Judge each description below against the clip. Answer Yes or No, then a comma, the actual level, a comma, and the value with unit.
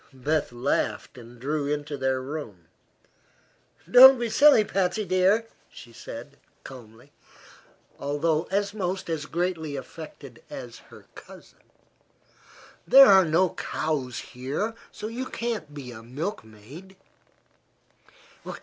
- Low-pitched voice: No, medium, 155 Hz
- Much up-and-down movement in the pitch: Yes, wide, 6.7 semitones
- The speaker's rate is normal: No, slow, 115 wpm